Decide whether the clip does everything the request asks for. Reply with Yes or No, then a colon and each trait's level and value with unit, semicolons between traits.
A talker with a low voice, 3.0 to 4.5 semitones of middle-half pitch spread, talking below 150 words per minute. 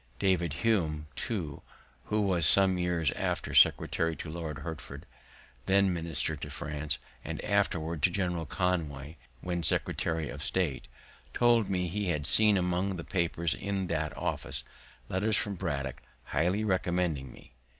Yes: very low, 85 Hz; average, 3.6 semitones; average, 140 wpm